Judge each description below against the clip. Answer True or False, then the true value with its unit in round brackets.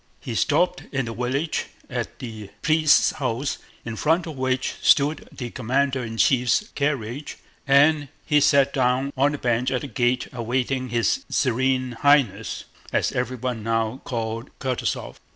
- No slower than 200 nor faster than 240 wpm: False (150 wpm)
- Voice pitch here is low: True (130 Hz)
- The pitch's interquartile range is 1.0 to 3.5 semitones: True (2.8 semitones)